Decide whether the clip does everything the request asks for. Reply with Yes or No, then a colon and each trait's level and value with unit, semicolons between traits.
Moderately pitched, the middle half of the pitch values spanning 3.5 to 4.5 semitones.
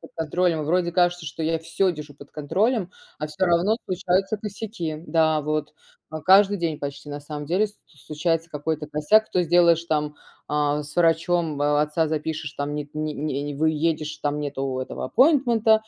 No: medium, 160 Hz; average, 3.1 semitones